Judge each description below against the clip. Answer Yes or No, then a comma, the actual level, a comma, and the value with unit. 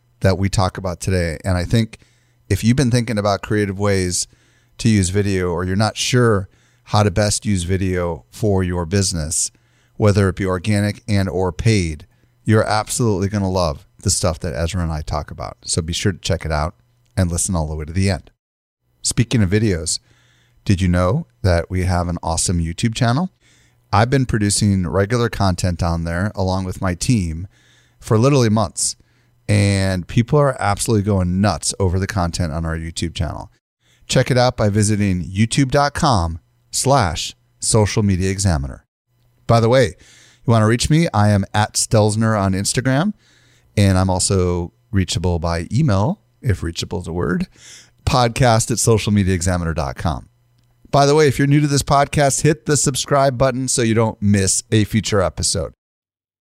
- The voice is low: Yes, low, 105 Hz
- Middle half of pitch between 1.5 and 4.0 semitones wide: No, average, 4.6 semitones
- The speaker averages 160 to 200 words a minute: Yes, average, 170 wpm